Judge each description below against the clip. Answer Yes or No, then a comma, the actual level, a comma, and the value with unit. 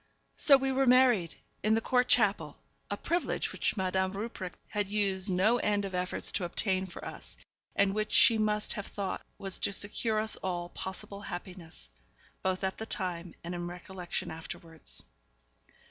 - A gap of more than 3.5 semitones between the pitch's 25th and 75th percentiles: No, average, 2.9 semitones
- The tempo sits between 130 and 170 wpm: Yes, average, 165 wpm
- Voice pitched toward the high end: Yes, high, 195 Hz